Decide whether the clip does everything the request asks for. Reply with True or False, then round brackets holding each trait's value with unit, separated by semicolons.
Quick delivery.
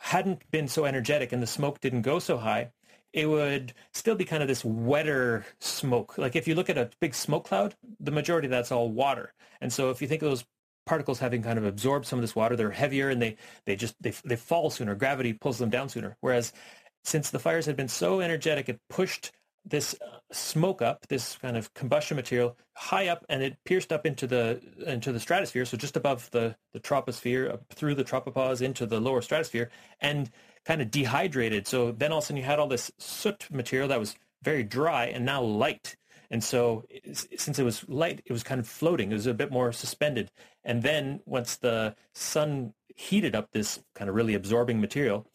True (215 wpm)